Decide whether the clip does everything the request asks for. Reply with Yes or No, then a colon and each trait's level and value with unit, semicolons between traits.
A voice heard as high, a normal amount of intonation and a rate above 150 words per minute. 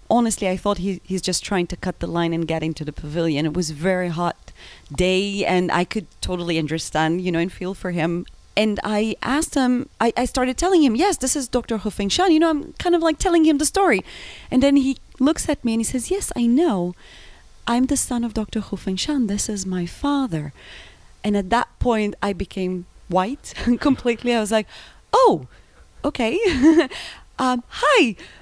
No: high, 220 Hz; wide, 6.7 semitones; fast, 205 wpm